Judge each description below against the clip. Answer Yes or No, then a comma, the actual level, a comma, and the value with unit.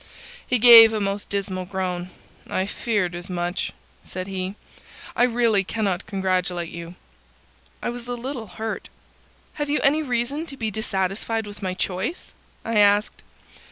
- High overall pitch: Yes, high, 205 Hz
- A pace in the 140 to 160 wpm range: Yes, average, 150 wpm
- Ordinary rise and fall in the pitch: Yes, average, 4.1 semitones